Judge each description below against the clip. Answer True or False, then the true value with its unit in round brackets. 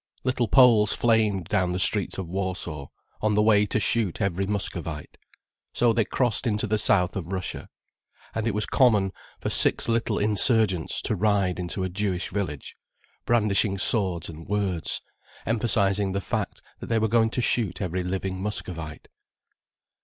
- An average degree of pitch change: True (3.1 semitones)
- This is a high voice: False (100 Hz)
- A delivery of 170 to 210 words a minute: False (160 wpm)